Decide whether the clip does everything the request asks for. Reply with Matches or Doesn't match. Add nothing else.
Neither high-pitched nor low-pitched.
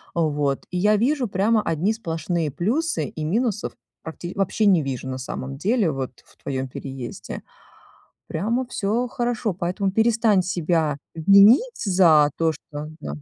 Matches